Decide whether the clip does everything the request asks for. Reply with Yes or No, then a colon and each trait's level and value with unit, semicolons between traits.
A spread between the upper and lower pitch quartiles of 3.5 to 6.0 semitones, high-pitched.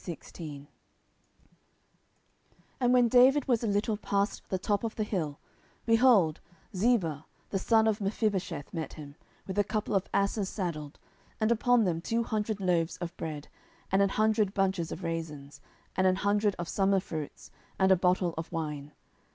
Yes: average, 4.6 semitones; high, 195 Hz